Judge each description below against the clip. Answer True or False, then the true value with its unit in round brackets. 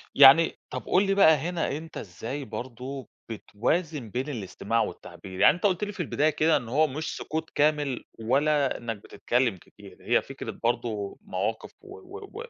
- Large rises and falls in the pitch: True (5.7 semitones)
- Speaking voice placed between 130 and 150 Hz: True (140 Hz)